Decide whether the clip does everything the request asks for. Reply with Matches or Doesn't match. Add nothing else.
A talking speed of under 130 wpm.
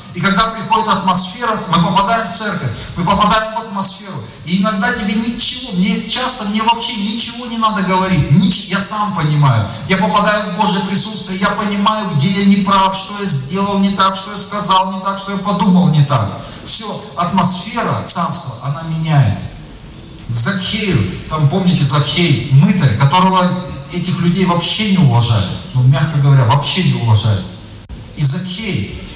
Doesn't match